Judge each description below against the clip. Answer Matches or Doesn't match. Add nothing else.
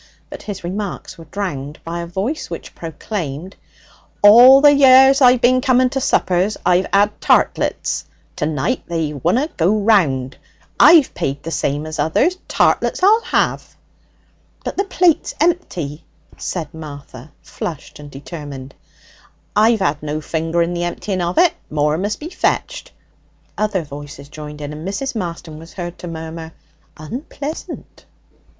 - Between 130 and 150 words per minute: Matches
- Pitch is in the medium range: Matches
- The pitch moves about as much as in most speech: Doesn't match